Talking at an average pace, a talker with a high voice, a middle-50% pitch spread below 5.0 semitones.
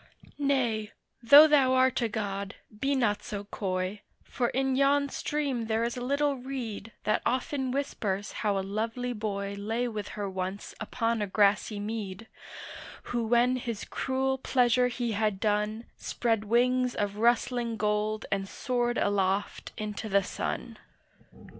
Yes: average, 145 wpm; high, 225 Hz; average, 3.5 semitones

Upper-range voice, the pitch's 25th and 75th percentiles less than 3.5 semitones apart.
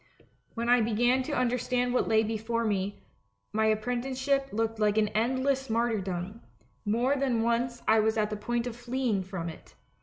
Yes: high, 230 Hz; narrow, 2.5 semitones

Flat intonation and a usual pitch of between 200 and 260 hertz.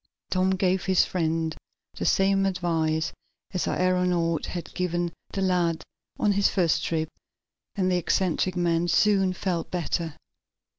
No: narrow, 2.0 semitones; medium, 180 Hz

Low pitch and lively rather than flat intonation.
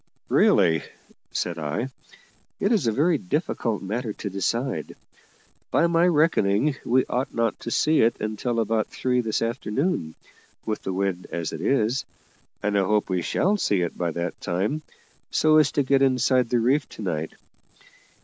Yes: low, 115 Hz; wide, 5.8 semitones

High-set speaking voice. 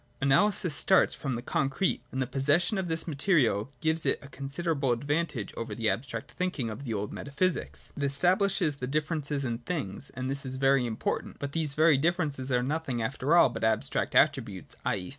No: medium, 140 Hz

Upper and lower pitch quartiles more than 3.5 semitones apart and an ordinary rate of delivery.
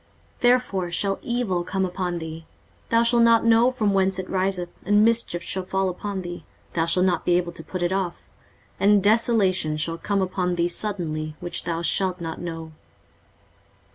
No: average, 2.9 semitones; average, 180 wpm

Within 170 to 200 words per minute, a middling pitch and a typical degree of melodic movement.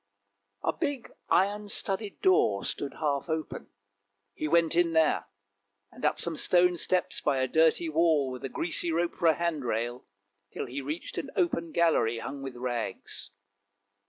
No: average, 160 wpm; medium, 160 Hz; average, 4.2 semitones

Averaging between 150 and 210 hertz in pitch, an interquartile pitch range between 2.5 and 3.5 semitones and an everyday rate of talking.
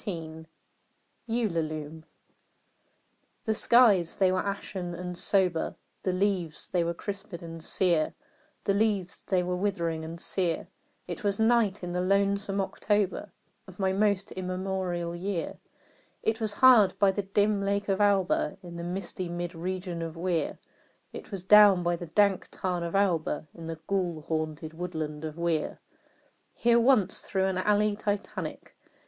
Yes: medium, 185 Hz; average, 2.9 semitones; average, 150 wpm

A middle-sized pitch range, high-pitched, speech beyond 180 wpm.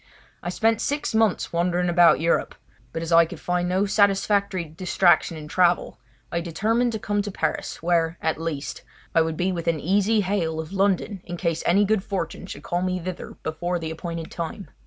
No: average, 3.0 semitones; medium, 175 Hz; average, 190 wpm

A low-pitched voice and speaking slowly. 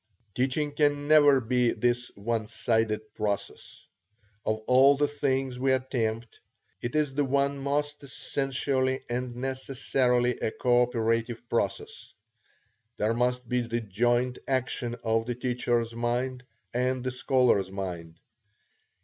Yes: low, 125 Hz; slow, 125 wpm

